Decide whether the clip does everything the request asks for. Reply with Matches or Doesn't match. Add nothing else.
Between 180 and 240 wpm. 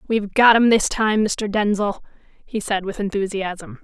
Doesn't match